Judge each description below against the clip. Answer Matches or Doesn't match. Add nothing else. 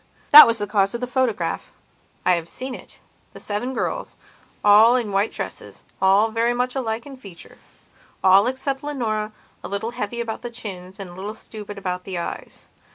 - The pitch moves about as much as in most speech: Matches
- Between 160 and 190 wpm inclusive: Matches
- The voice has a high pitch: Matches